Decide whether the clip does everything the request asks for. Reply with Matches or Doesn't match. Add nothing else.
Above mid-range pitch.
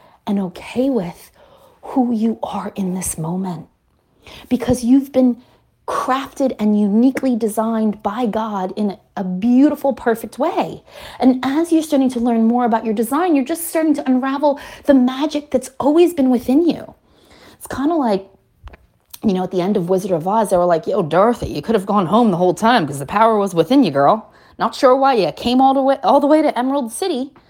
Matches